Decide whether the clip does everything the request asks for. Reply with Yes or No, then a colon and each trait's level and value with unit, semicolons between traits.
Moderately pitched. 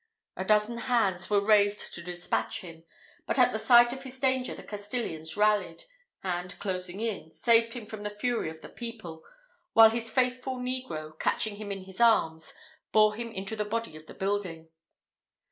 No: high, 210 Hz